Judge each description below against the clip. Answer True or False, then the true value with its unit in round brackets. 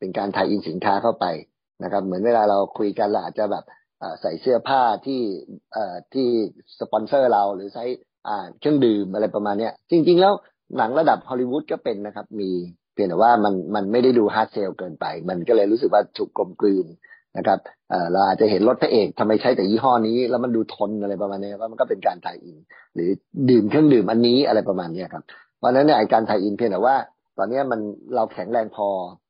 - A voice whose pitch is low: True (115 Hz)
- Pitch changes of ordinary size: True (4.0 semitones)